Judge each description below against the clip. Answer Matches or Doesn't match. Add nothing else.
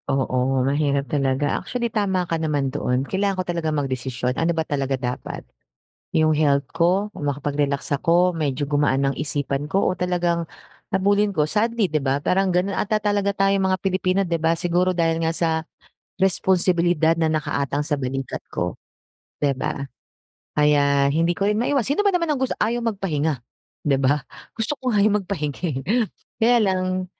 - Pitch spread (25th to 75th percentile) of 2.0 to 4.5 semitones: Doesn't match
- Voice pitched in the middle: Matches